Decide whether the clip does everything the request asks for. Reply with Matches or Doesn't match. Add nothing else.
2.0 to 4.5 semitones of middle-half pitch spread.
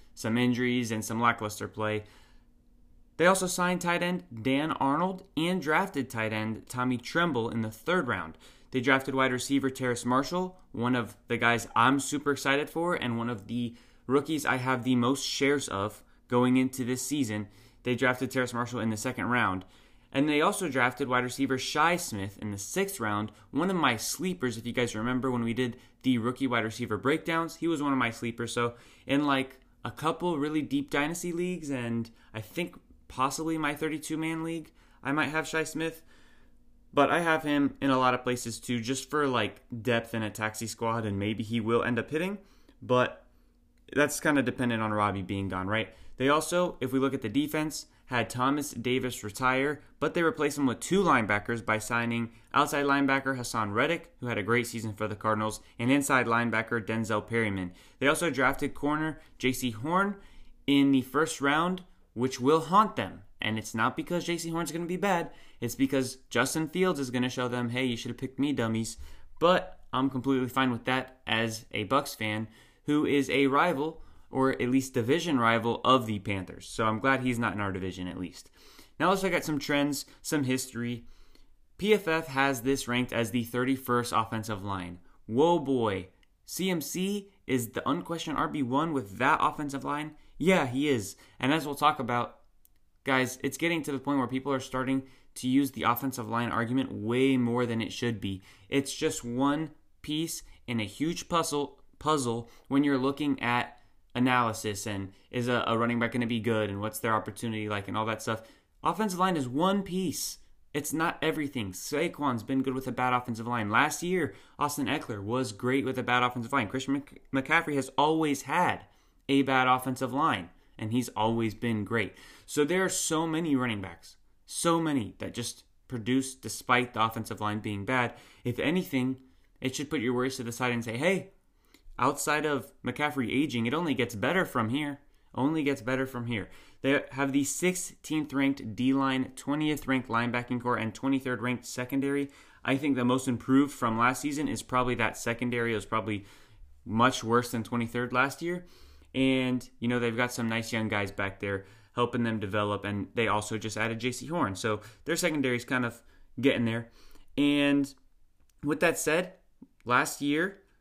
Matches